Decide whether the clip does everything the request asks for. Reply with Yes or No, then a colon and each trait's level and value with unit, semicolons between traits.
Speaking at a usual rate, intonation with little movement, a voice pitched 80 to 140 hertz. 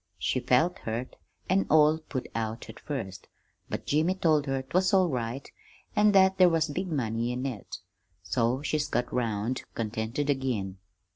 No: average, 160 wpm; wide, 5.5 semitones; low, 135 Hz